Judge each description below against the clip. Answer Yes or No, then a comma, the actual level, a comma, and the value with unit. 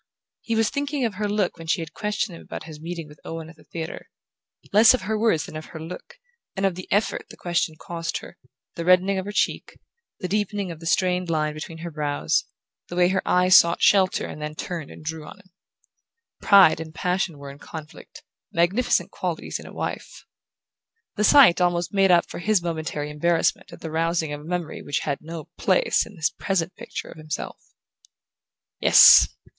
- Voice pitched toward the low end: No, medium, 175 Hz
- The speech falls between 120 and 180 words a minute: No, fast, 205 wpm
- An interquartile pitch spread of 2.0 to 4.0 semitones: Yes, average, 3.5 semitones